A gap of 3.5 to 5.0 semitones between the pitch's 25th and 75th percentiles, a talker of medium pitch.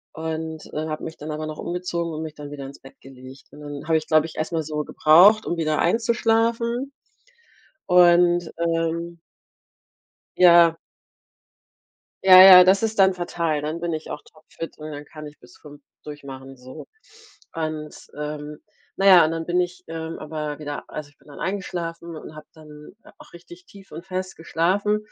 No: average, 2.8 semitones; medium, 160 Hz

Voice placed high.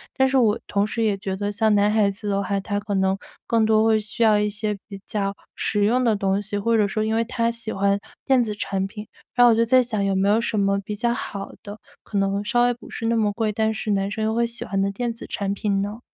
Yes: high, 210 Hz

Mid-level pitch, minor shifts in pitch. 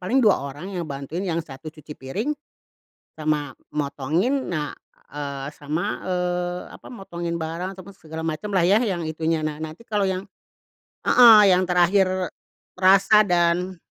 No: medium, 175 Hz; average, 3.7 semitones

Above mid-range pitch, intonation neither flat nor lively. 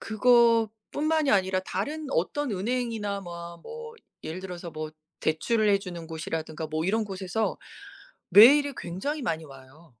No: high, 195 Hz; wide, 5.7 semitones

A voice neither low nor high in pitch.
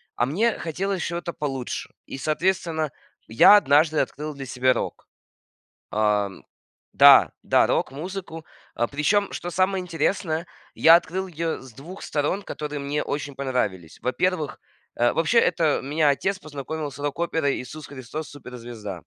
Yes: medium, 150 Hz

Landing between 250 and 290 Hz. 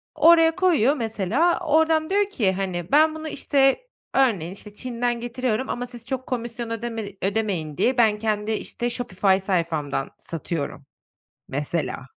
No: high, 235 Hz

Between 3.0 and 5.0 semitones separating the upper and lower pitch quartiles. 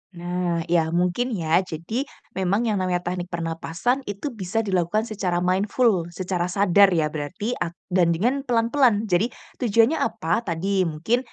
Yes: average, 4.3 semitones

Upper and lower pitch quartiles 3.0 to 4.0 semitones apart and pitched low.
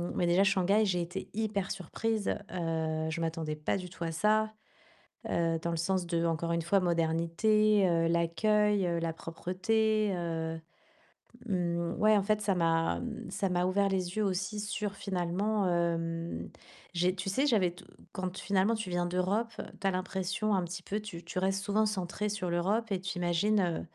No: average, 3.3 semitones; medium, 185 Hz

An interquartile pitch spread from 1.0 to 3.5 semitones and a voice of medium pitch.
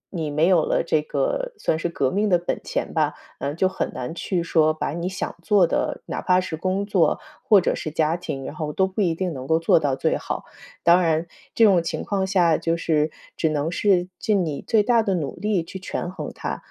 Yes: average, 3.2 semitones; medium, 170 Hz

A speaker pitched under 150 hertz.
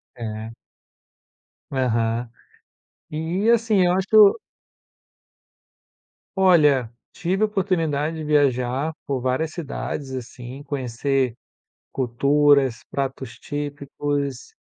Yes: medium, 140 Hz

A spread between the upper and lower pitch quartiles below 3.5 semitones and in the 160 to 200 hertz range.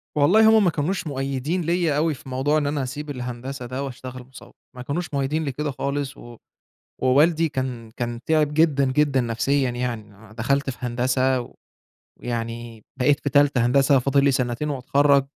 No: average, 2.9 semitones; low, 135 Hz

